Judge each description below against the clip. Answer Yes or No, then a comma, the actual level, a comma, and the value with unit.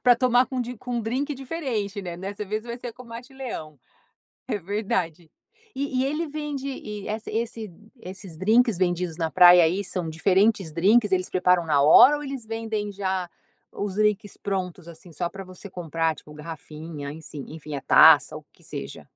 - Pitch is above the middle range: Yes, high, 200 Hz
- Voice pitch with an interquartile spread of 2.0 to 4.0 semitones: No, wide, 5.5 semitones